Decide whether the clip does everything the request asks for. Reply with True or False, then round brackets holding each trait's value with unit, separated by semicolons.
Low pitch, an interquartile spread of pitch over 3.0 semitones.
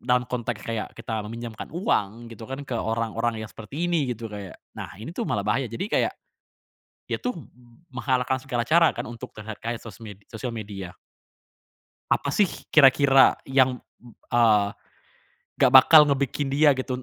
True (120 Hz; 3.5 semitones)